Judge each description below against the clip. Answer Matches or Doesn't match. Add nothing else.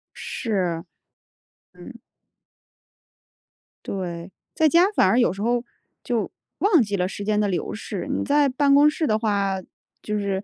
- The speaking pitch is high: Matches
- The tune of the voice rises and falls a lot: Matches